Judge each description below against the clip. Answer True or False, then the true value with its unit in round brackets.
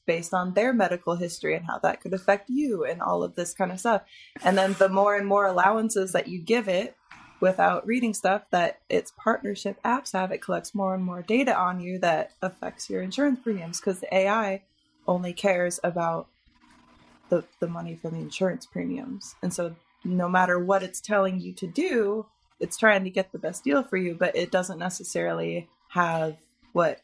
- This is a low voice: False (190 Hz)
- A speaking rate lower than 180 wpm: False (195 wpm)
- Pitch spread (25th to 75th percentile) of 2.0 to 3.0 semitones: True (2.5 semitones)